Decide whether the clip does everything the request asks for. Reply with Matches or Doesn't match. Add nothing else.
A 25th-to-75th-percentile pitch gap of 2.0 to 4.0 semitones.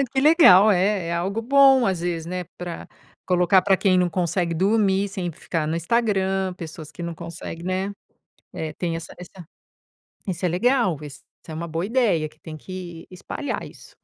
Matches